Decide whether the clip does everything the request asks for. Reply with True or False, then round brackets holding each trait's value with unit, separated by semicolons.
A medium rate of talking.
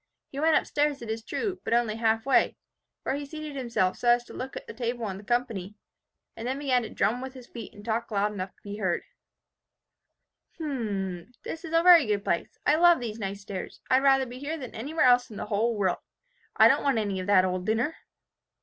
False (240 wpm)